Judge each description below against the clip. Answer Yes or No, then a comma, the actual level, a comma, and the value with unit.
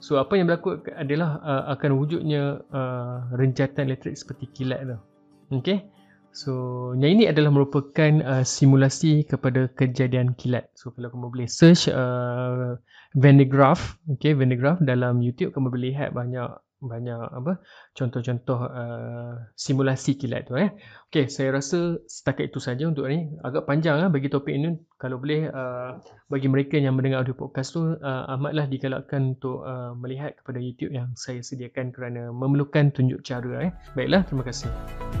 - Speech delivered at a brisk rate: Yes, fast, 165 wpm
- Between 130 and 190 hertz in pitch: Yes, low, 135 Hz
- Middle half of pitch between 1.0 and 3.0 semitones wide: Yes, average, 2.7 semitones